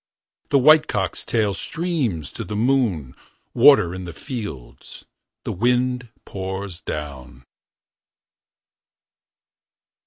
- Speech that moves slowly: Yes, slow, 95 wpm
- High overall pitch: No, low, 100 Hz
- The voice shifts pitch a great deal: Yes, wide, 7.1 semitones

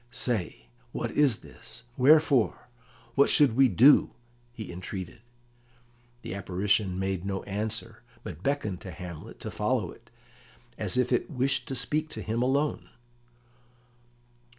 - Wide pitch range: Yes, wide, 5.7 semitones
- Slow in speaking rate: Yes, slow, 130 wpm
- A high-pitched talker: No, low, 115 Hz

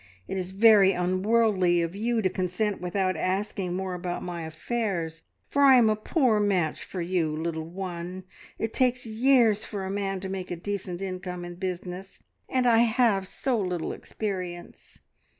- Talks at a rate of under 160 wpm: No, average, 170 wpm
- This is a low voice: No, high, 190 Hz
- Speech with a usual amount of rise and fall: Yes, average, 3.4 semitones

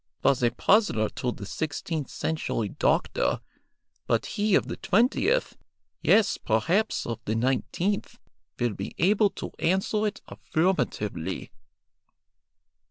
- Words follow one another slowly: Yes, slow, 115 wpm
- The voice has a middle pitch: Yes, medium, 160 Hz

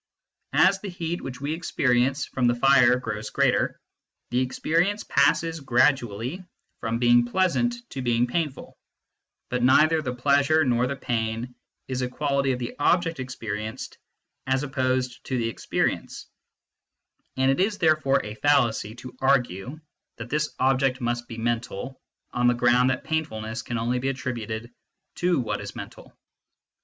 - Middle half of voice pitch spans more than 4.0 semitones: No, average, 3.3 semitones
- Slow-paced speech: No, average, 150 wpm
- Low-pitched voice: Yes, low, 130 Hz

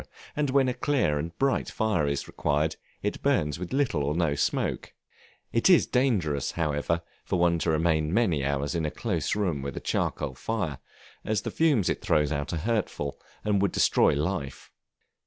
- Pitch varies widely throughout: Yes, wide, 6.9 semitones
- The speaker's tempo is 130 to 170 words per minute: No, average, 185 wpm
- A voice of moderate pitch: No, very low, 85 Hz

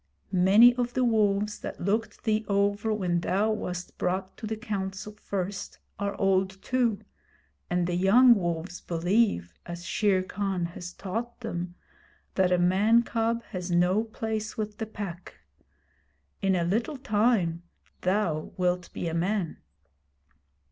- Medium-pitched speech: No, high, 195 Hz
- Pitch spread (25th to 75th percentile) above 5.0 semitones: No, average, 3.5 semitones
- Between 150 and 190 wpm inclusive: No, average, 140 wpm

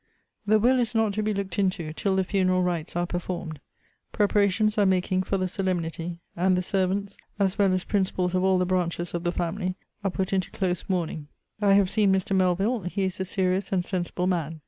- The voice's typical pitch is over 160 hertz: Yes, medium, 185 Hz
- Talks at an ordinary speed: No, fast, 210 wpm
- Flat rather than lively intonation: Yes, narrow, 1.9 semitones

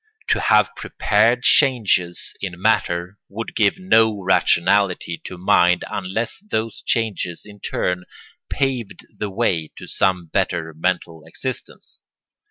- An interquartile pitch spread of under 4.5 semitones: Yes, average, 4.1 semitones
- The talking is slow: Yes, slow, 120 wpm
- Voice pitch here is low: Yes, low, 100 Hz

